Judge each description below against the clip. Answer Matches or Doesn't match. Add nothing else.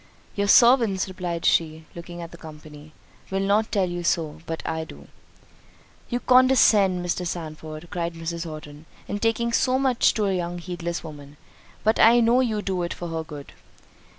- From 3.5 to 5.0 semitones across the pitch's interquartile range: Matches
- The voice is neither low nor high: Matches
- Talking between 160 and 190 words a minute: Matches